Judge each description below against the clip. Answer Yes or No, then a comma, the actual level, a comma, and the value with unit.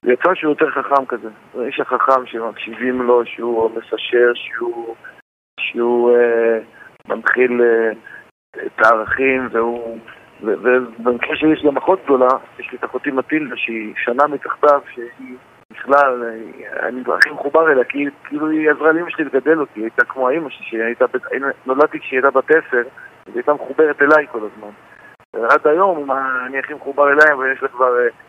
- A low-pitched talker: Yes, low, 130 Hz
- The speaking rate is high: Yes, fast, 170 wpm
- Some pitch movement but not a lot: Yes, average, 3.7 semitones